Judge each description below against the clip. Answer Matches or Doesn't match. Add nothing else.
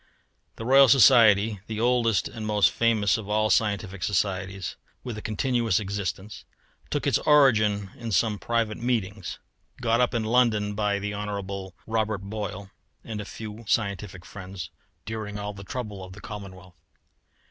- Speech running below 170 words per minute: Matches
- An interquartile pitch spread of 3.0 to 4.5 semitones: Doesn't match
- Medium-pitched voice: Doesn't match